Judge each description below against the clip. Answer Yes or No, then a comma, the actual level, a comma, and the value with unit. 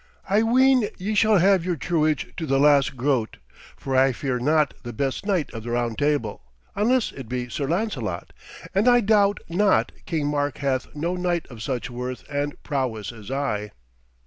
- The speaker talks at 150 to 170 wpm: No, average, 180 wpm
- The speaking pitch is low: No, medium, 145 Hz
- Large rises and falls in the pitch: Yes, wide, 6.8 semitones